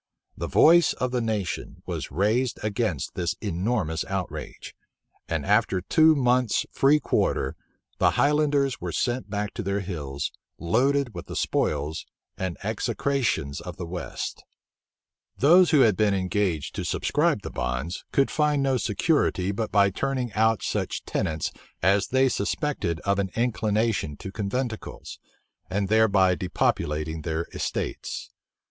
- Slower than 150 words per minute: Yes, average, 140 wpm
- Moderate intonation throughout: No, wide, 5.8 semitones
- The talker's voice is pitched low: Yes, low, 105 Hz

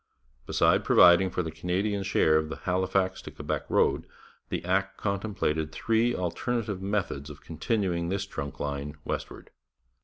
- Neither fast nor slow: Yes, average, 145 wpm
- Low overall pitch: Yes, very low, 95 Hz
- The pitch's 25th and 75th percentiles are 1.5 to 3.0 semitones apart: No, average, 3.8 semitones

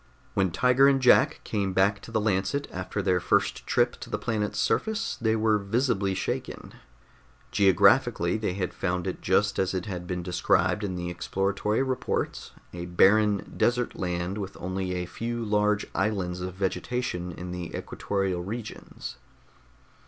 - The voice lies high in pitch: No, very low, 95 Hz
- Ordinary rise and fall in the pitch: Yes, average, 3.3 semitones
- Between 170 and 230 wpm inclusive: No, average, 155 wpm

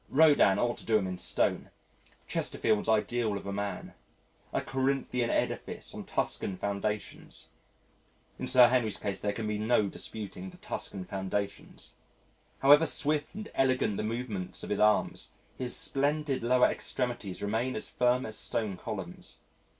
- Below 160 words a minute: Yes, average, 150 wpm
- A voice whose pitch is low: Yes, low, 110 Hz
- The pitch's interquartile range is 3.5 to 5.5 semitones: Yes, average, 4.0 semitones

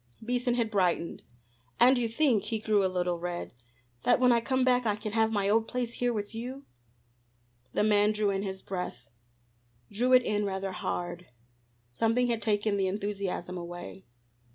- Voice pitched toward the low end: No, high, 210 Hz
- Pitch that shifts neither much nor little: Yes, average, 3.7 semitones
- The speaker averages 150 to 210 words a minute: Yes, average, 175 wpm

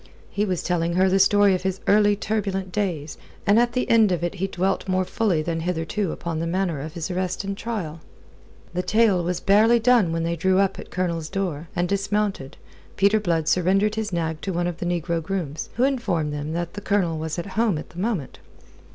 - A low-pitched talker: No, medium, 185 Hz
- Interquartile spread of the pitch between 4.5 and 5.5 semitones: No, average, 3.4 semitones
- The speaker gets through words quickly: Yes, fast, 220 wpm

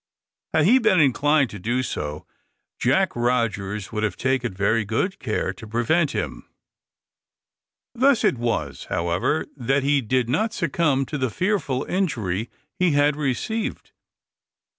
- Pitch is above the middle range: No, low, 130 Hz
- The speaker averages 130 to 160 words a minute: Yes, average, 140 wpm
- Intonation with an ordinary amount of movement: No, wide, 6.0 semitones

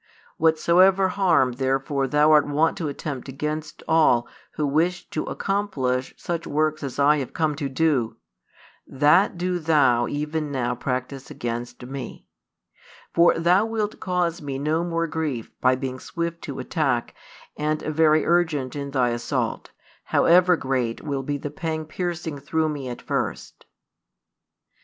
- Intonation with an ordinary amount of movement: Yes, average, 3.7 semitones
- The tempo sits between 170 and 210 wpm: No, average, 145 wpm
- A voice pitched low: No, medium, 150 Hz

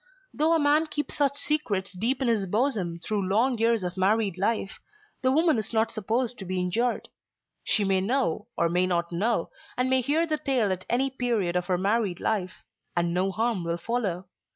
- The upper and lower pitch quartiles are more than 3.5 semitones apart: Yes, wide, 5.5 semitones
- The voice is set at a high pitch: Yes, high, 220 Hz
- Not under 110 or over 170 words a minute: No, average, 200 wpm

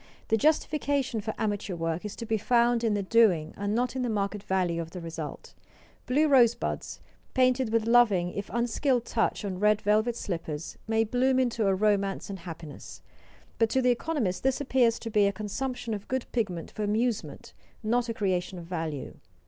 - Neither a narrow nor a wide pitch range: Yes, average, 4.2 semitones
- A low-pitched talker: No, high, 215 Hz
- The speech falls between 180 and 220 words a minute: Yes, average, 185 wpm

